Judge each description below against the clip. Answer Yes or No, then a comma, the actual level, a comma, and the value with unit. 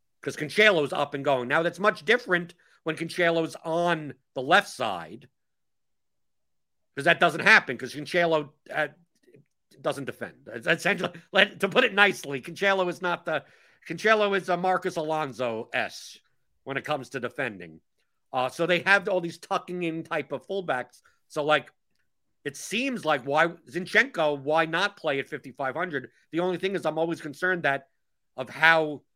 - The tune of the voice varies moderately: Yes, average, 4.0 semitones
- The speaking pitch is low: No, medium, 165 Hz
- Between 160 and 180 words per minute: Yes, average, 165 wpm